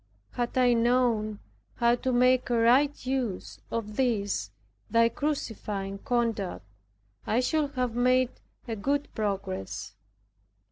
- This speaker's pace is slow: Yes, slow, 120 wpm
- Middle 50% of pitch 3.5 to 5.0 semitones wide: No, average, 3.1 semitones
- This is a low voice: No, high, 240 Hz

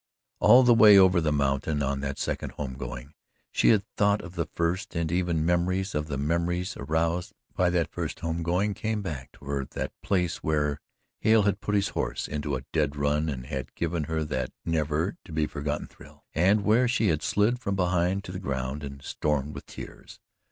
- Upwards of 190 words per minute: Yes, average, 200 wpm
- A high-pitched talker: No, very low, 85 Hz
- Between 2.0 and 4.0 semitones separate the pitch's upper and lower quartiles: No, average, 4.5 semitones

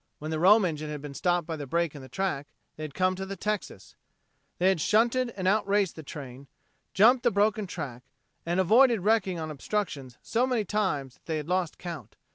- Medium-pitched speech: Yes, medium, 180 Hz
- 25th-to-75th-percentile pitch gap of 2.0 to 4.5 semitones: No, wide, 5.5 semitones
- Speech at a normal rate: No, fast, 210 wpm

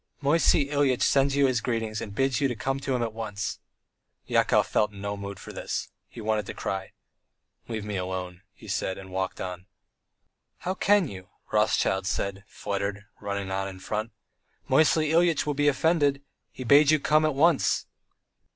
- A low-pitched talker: Yes, low, 115 Hz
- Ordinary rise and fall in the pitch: No, wide, 6.1 semitones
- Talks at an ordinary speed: Yes, average, 175 wpm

